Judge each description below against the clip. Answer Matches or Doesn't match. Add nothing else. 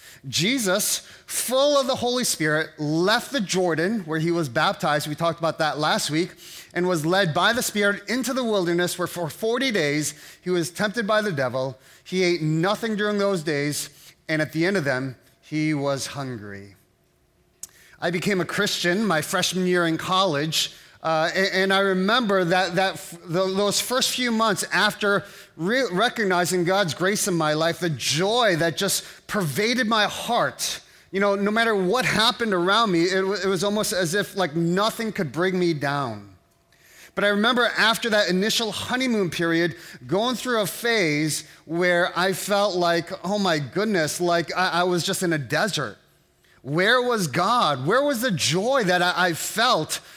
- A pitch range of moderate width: Matches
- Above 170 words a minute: Matches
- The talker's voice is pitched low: Doesn't match